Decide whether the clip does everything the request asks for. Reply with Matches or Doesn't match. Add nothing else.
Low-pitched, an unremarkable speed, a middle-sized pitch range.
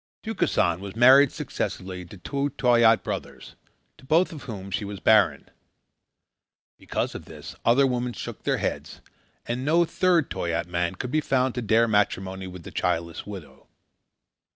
Doesn't match